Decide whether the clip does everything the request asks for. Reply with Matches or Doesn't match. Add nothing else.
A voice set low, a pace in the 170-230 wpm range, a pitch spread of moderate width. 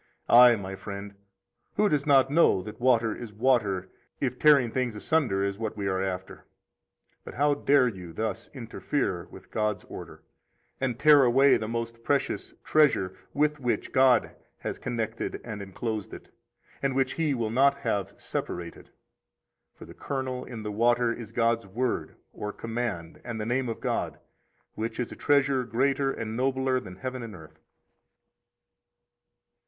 Doesn't match